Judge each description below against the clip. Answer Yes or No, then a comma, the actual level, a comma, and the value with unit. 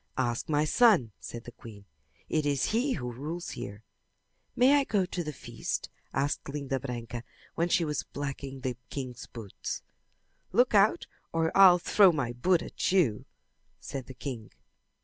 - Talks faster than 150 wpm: Yes, average, 160 wpm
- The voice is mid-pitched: Yes, medium, 145 Hz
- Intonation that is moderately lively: No, wide, 6.3 semitones